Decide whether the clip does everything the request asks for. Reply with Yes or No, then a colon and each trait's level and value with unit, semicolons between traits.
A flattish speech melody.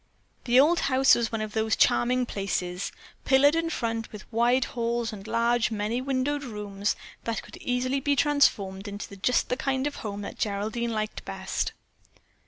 No: average, 3.7 semitones